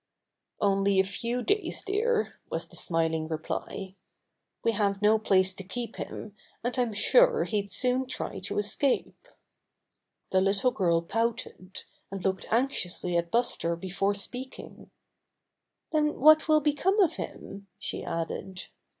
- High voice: Yes, high, 205 Hz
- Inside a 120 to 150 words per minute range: Yes, slow, 135 wpm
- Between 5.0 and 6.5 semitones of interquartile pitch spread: Yes, average, 5.3 semitones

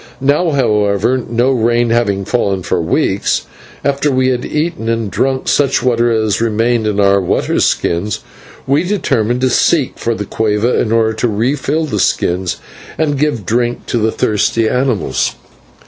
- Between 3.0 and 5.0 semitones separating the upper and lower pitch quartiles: Yes, average, 3.7 semitones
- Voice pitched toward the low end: Yes, low, 115 Hz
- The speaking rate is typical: Yes, average, 160 wpm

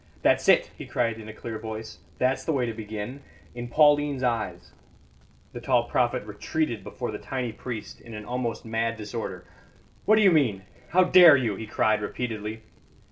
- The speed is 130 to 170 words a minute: No, average, 185 wpm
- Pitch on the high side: No, low, 115 Hz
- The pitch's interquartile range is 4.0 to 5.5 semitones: No, average, 3.1 semitones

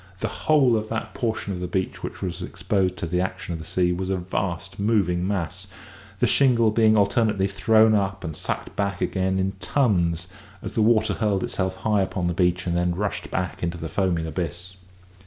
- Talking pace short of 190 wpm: No, average, 200 wpm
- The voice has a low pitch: Yes, very low, 95 Hz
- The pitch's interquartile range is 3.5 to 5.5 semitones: No, average, 3.1 semitones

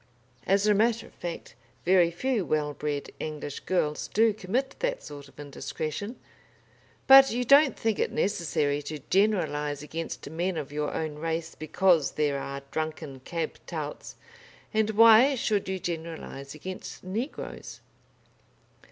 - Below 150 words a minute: Yes, average, 140 wpm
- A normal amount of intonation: No, wide, 6.1 semitones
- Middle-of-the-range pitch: Yes, medium, 170 Hz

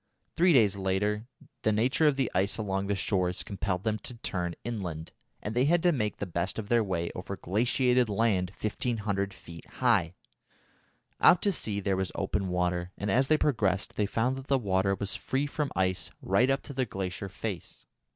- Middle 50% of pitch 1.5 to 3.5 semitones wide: No, average, 4.6 semitones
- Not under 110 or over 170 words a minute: No, average, 190 wpm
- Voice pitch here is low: Yes, low, 105 Hz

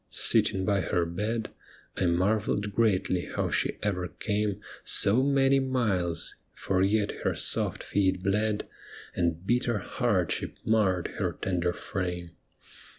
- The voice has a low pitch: Yes, low, 100 Hz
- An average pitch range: Yes, average, 3.3 semitones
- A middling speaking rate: No, slow, 125 wpm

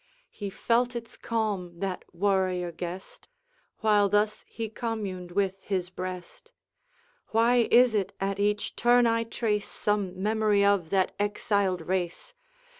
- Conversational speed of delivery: No, slow, 130 wpm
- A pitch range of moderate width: Yes, average, 3.1 semitones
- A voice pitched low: No, high, 205 Hz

